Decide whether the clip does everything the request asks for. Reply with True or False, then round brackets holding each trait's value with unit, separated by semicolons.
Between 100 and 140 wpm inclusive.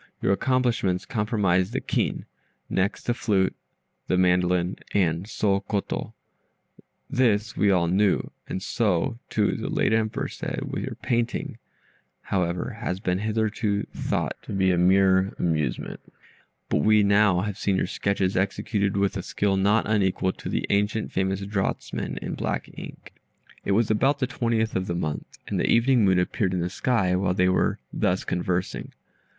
False (155 wpm)